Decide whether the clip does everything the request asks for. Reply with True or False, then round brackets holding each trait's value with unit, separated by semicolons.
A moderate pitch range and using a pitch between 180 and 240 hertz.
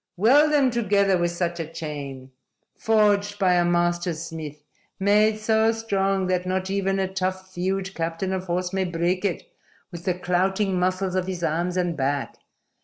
False (2.2 semitones; 185 Hz)